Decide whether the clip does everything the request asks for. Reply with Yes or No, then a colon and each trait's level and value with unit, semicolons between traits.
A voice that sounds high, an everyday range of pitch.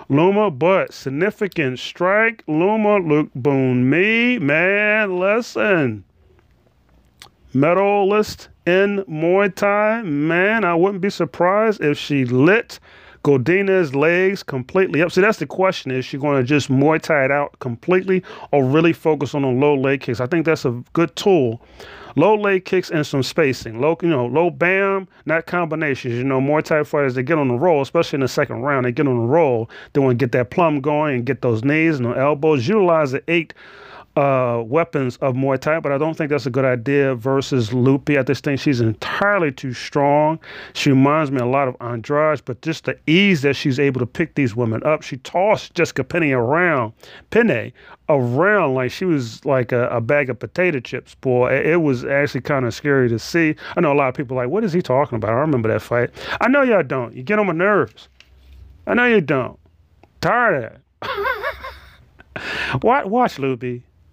No: medium, 145 Hz; average, 5.0 semitones